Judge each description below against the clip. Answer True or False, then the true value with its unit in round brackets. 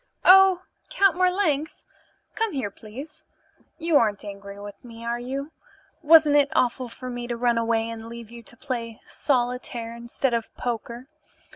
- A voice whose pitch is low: False (245 Hz)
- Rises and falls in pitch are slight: False (4.1 semitones)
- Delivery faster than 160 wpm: False (155 wpm)